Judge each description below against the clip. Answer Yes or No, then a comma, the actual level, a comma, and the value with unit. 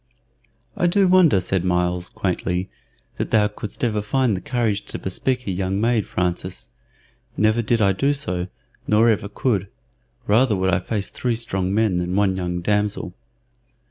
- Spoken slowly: No, average, 165 wpm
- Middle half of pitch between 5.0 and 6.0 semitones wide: No, average, 3.8 semitones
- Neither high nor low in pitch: No, low, 105 Hz